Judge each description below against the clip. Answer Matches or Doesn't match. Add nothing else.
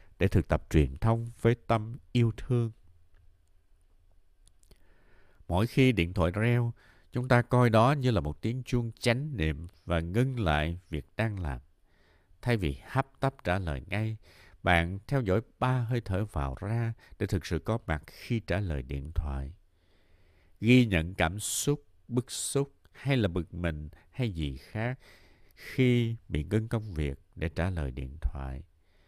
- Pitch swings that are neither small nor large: Doesn't match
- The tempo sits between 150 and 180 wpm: Matches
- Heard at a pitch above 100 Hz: Doesn't match